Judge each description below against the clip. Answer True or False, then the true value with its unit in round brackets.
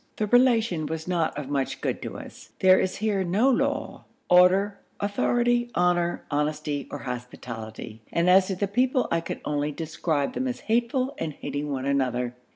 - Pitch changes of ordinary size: False (6.6 semitones)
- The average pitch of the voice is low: False (175 Hz)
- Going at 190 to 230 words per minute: False (170 wpm)